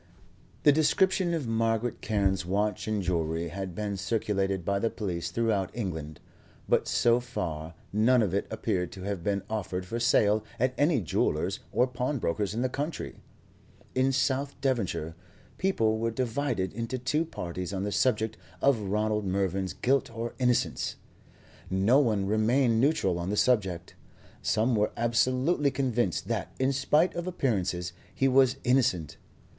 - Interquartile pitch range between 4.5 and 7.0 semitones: Yes, average, 5.1 semitones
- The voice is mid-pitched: No, low, 110 Hz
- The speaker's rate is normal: Yes, average, 150 wpm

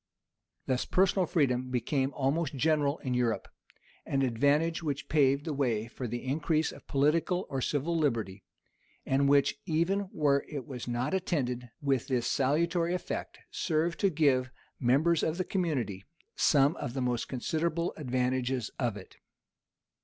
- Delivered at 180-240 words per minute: No, average, 150 wpm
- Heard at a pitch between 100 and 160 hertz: Yes, medium, 140 Hz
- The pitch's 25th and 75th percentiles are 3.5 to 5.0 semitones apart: Yes, average, 4.1 semitones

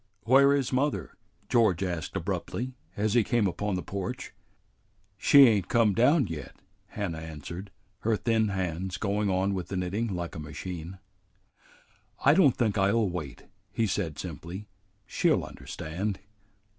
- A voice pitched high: No, low, 100 Hz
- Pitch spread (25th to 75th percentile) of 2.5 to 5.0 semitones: Yes, average, 4.5 semitones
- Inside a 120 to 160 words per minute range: Yes, average, 145 wpm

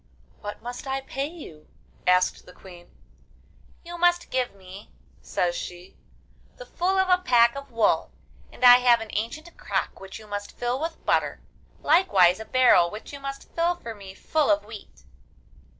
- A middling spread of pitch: No, wide, 6.5 semitones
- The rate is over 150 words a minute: Yes, average, 170 wpm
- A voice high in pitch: Yes, high, 240 Hz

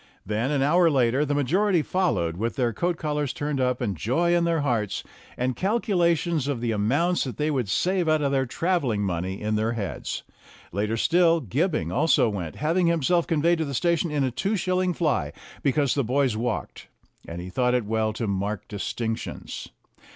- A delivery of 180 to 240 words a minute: Yes, average, 190 wpm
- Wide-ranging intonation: Yes, wide, 7.0 semitones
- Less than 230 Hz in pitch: Yes, medium, 140 Hz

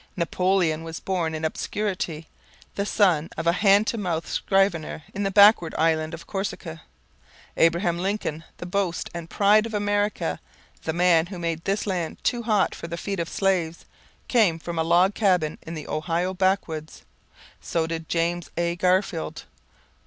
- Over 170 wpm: No, average, 160 wpm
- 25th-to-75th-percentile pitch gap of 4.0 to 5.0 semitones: No, average, 3.2 semitones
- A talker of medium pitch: Yes, medium, 175 Hz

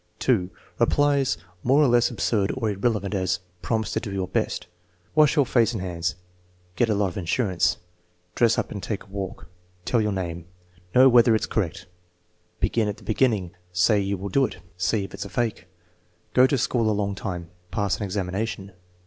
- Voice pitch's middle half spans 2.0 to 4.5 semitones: Yes, average, 4.0 semitones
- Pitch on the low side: Yes, low, 105 Hz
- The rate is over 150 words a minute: Yes, average, 190 wpm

